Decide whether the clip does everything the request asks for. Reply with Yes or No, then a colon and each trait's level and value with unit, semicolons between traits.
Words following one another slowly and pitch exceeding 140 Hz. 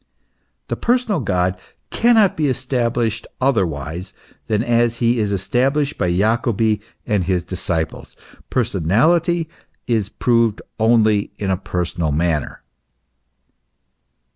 No: slow, 105 wpm; low, 110 Hz